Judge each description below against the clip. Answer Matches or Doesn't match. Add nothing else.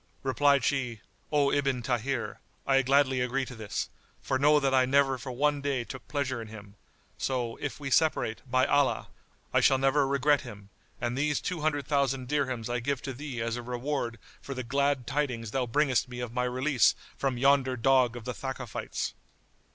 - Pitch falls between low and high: Doesn't match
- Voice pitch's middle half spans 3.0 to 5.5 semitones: Doesn't match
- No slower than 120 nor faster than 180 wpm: Doesn't match